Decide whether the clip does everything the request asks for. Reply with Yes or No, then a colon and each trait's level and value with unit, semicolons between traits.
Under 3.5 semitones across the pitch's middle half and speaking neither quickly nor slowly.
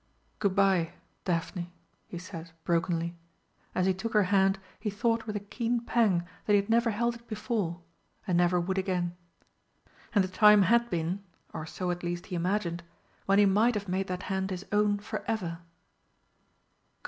Yes: average, 3.0 semitones; average, 175 wpm